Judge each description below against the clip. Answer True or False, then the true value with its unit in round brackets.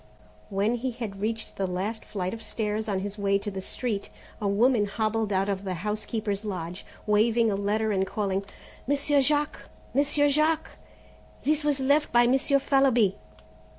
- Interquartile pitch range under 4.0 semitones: False (4.8 semitones)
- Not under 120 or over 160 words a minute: False (170 wpm)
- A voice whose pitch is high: True (215 Hz)